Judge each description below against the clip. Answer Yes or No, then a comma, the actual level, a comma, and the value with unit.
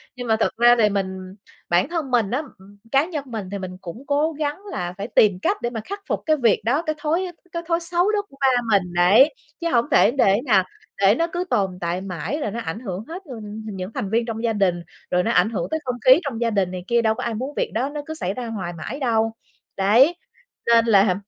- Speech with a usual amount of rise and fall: No, wide, 6.4 semitones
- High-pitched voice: Yes, high, 230 Hz